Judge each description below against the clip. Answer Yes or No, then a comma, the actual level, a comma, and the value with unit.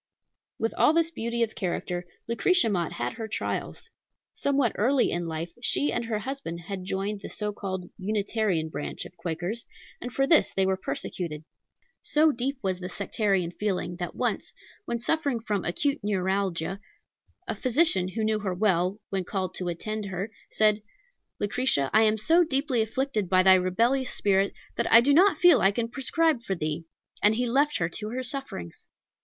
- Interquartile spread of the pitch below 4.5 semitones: No, average, 5.1 semitones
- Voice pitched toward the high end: Yes, high, 210 Hz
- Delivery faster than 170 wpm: Yes, average, 180 wpm